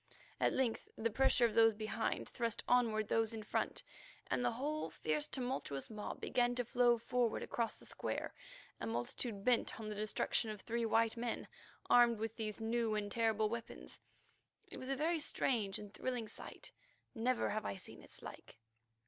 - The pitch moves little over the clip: Yes, narrow, 2.3 semitones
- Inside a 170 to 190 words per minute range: Yes, average, 175 wpm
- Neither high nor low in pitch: No, high, 225 Hz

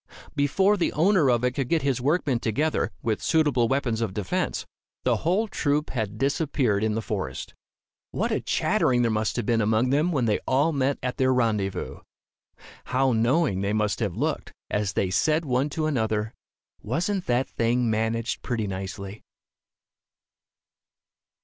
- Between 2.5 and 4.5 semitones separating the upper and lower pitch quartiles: No, average, 4.9 semitones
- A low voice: Yes, low, 125 Hz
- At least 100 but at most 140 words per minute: No, average, 160 wpm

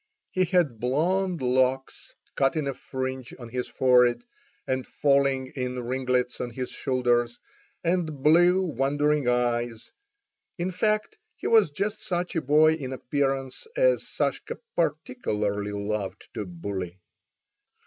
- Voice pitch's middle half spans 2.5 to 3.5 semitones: No, average, 4.7 semitones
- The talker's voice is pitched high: No, low, 130 Hz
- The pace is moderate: No, slow, 130 wpm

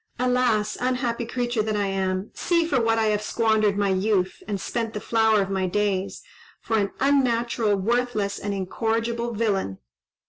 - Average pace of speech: Yes, average, 165 wpm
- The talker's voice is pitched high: Yes, high, 220 Hz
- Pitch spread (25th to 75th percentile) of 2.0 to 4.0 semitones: Yes, average, 2.9 semitones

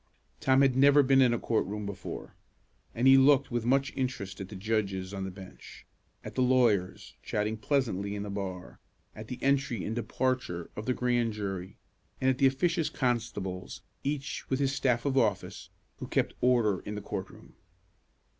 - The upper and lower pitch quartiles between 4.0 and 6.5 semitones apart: Yes, average, 4.6 semitones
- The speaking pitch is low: Yes, low, 120 Hz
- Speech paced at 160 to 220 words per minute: Yes, average, 185 wpm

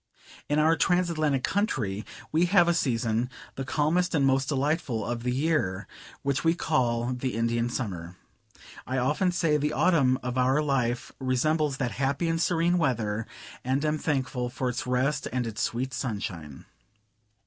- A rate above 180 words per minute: No, average, 160 wpm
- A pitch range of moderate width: Yes, average, 4.2 semitones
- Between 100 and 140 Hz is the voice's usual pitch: Yes, low, 135 Hz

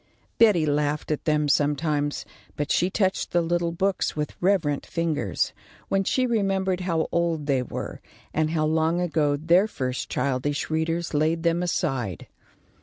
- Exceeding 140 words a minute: Yes, average, 150 wpm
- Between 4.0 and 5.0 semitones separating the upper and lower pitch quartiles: No, average, 3.1 semitones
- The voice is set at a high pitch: No, medium, 160 Hz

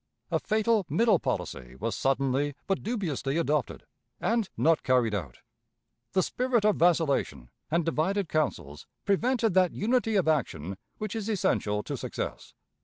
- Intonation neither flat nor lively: No, wide, 7.8 semitones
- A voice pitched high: No, medium, 170 Hz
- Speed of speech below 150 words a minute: Yes, average, 140 wpm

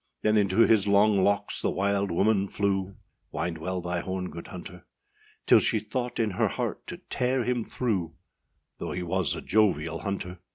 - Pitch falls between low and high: No, low, 100 Hz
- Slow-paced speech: No, average, 180 wpm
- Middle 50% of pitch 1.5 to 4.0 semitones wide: Yes, average, 3.1 semitones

